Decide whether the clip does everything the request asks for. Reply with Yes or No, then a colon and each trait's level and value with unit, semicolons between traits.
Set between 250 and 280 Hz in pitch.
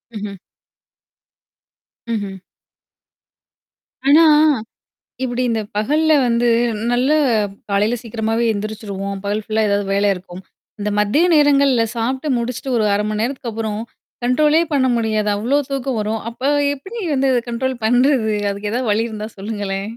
No: high, 225 Hz